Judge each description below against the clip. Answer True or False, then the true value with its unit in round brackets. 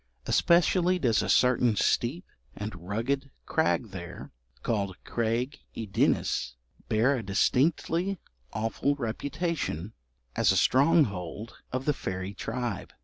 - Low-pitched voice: True (120 Hz)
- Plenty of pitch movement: True (6.0 semitones)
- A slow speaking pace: True (115 wpm)